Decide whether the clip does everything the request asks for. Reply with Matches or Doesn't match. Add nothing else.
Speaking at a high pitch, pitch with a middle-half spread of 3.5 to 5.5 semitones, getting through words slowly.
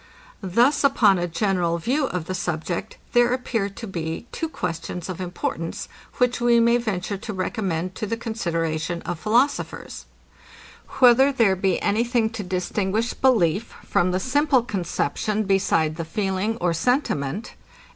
Doesn't match